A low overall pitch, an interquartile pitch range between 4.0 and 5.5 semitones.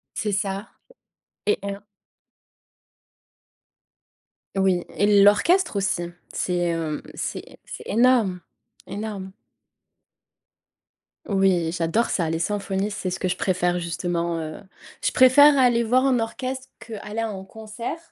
No: high, 200 Hz; average, 4.3 semitones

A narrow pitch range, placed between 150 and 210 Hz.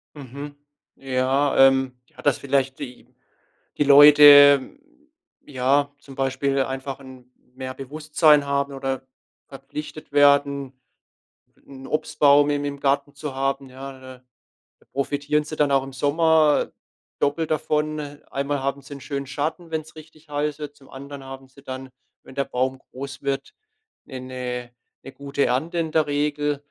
No: narrow, 1.6 semitones; medium, 140 Hz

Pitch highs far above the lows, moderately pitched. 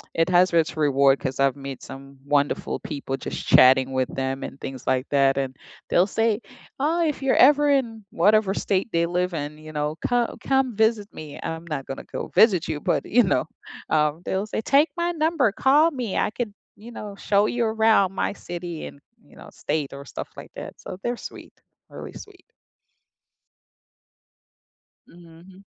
Yes: wide, 7.9 semitones; medium, 180 Hz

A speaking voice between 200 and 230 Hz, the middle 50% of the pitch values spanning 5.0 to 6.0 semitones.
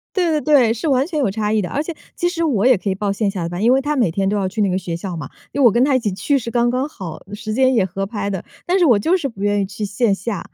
Yes: high, 220 Hz; wide, 5.5 semitones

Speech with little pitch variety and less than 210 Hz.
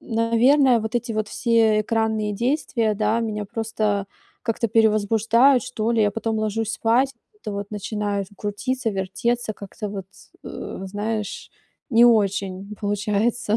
No: narrow, 2.0 semitones; high, 220 Hz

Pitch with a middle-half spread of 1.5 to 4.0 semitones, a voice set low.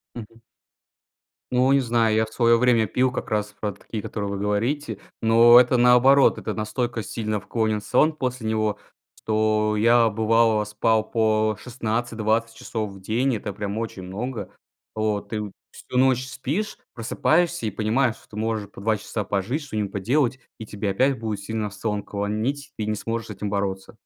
Yes: narrow, 2.6 semitones; low, 110 Hz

